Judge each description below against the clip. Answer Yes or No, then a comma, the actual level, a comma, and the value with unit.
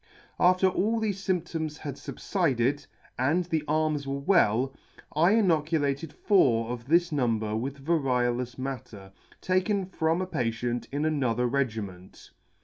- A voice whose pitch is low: No, medium, 145 Hz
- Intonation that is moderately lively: No, wide, 5.7 semitones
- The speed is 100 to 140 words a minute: Yes, slow, 135 wpm